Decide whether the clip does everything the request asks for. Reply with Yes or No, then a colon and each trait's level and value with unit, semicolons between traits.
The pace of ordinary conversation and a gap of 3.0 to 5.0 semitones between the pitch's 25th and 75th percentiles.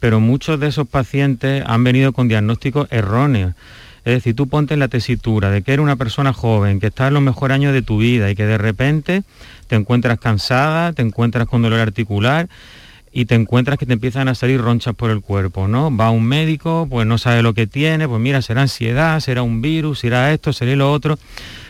No: fast, 215 wpm; average, 3.5 semitones